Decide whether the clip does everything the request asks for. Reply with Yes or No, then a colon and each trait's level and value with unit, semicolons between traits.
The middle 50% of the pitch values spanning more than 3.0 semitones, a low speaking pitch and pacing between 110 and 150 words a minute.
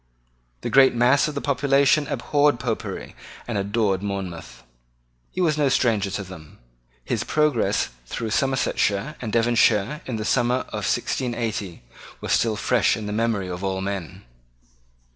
Yes: average, 5.0 semitones; low, 115 Hz; average, 145 wpm